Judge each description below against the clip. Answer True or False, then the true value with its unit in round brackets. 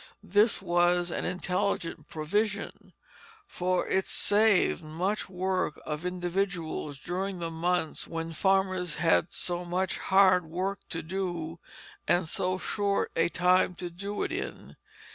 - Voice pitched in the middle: True (180 Hz)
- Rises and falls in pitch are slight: True (2.2 semitones)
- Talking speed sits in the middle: False (130 wpm)